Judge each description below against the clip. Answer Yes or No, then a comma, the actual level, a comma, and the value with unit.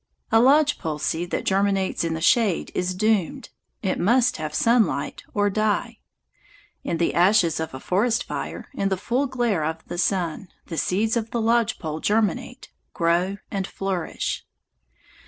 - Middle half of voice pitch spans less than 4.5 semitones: No, average, 4.8 semitones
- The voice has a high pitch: Yes, high, 195 Hz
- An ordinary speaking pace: Yes, average, 160 wpm